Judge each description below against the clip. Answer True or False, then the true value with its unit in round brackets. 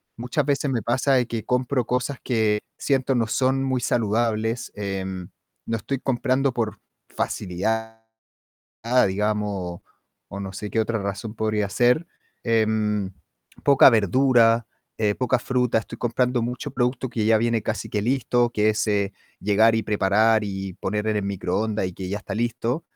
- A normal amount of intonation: True (3.0 semitones)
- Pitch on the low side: True (110 Hz)